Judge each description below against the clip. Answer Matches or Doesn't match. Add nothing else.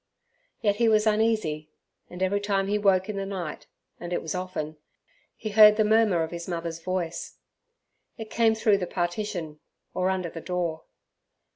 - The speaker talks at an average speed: Matches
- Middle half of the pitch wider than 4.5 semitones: Doesn't match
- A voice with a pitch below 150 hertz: Doesn't match